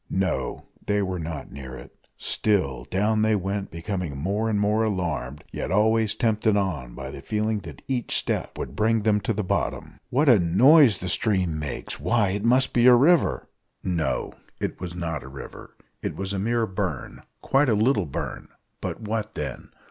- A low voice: Yes, low, 105 Hz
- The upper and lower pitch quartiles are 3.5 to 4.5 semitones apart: Yes, average, 4.2 semitones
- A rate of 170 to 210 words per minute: Yes, average, 185 wpm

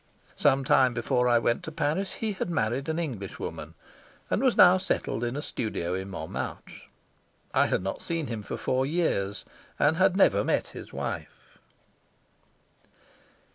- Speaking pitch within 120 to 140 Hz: Yes, low, 135 Hz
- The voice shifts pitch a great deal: Yes, wide, 6.7 semitones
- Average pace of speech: Yes, average, 155 wpm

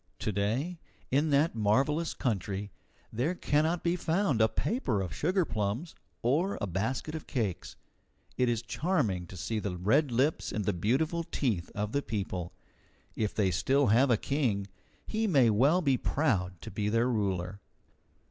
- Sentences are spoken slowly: No, average, 160 wpm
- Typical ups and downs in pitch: No, wide, 6.8 semitones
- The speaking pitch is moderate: No, low, 120 Hz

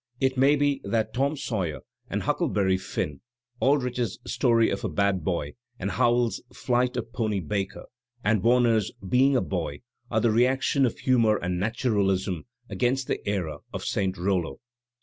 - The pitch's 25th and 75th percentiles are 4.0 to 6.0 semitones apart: Yes, average, 4.7 semitones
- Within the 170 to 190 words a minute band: No, average, 155 wpm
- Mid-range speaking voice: No, low, 110 Hz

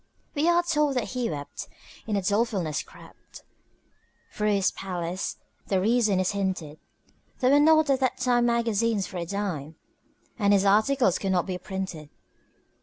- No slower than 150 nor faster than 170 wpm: Yes, average, 160 wpm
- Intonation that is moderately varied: Yes, average, 4.9 semitones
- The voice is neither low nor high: No, high, 205 Hz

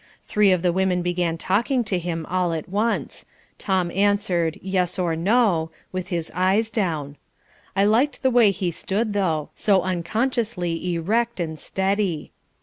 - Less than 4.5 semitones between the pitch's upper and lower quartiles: Yes, average, 3.4 semitones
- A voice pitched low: No, medium, 185 Hz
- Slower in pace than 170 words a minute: Yes, average, 150 wpm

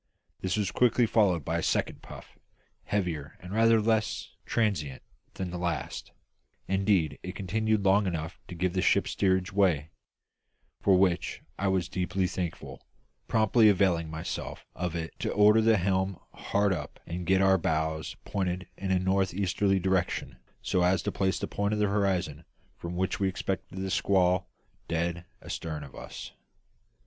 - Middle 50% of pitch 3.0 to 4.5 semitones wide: No, narrow, 2.4 semitones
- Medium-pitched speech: No, very low, 95 Hz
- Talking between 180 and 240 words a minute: No, average, 160 wpm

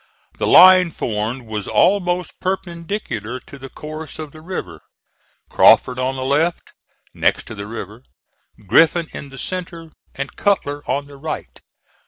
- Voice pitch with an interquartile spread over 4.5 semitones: Yes, average, 5.2 semitones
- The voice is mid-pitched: Yes, medium, 145 Hz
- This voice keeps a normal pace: Yes, average, 145 wpm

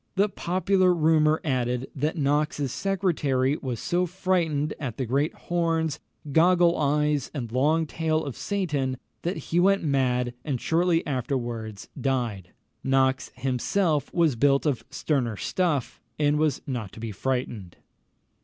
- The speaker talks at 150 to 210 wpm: No, slow, 135 wpm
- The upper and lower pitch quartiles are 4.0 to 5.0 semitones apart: Yes, average, 4.3 semitones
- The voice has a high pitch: No, medium, 145 Hz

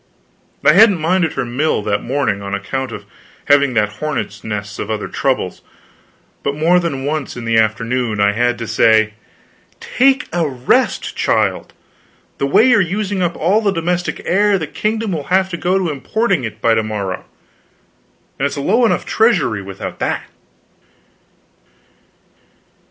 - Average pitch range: No, wide, 8.5 semitones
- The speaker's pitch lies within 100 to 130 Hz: No, medium, 140 Hz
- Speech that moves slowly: No, average, 160 wpm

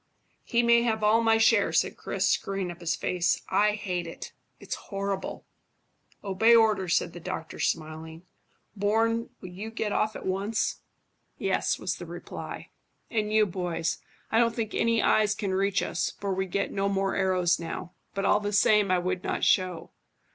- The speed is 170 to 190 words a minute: Yes, average, 175 wpm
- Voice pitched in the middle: No, high, 200 Hz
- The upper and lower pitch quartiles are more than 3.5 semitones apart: No, average, 3.1 semitones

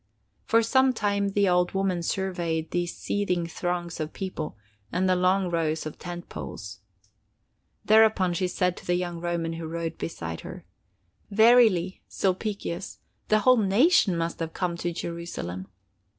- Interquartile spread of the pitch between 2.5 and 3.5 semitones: Yes, average, 2.9 semitones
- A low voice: No, medium, 180 Hz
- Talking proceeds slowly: No, average, 150 wpm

